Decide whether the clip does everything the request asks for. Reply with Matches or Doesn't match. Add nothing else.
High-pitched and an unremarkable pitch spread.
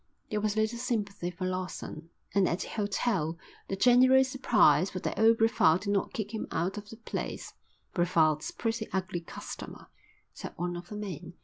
Matches